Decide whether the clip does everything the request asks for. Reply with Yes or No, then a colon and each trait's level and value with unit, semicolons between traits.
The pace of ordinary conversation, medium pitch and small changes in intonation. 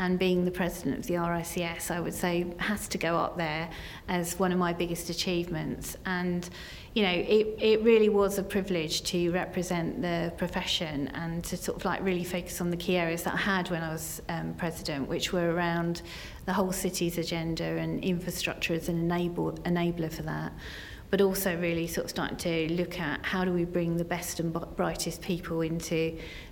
Yes: average, 195 wpm; medium, 175 Hz; narrow, 1.6 semitones